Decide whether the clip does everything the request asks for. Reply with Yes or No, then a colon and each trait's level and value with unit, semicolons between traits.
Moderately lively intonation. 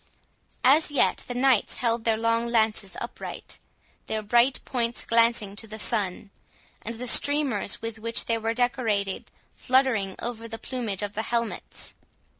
No: narrow, 2.1 semitones